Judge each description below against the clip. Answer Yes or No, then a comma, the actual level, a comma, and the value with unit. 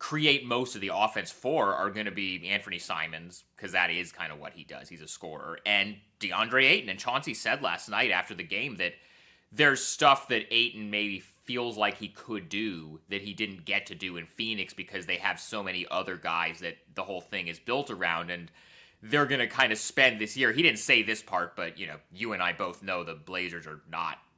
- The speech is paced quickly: Yes, fast, 230 wpm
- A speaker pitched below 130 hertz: Yes, low, 100 Hz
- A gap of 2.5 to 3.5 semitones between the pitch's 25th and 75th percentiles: No, average, 4.0 semitones